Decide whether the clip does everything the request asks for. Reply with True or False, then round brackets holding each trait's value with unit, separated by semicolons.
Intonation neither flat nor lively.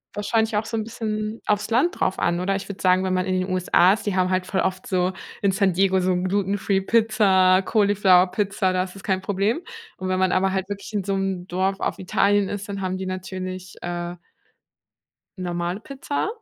False (1.7 semitones)